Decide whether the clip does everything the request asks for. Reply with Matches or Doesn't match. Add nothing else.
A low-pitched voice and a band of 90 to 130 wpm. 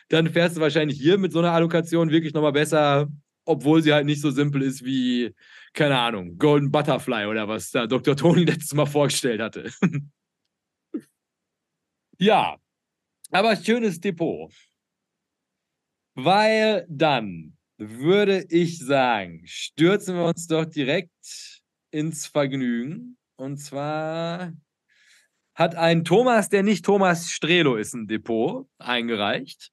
Doesn't match